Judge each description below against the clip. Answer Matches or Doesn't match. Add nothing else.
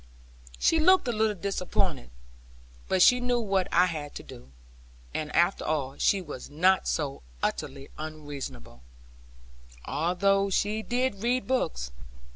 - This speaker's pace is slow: Matches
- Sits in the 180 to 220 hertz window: Matches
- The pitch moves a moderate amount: Doesn't match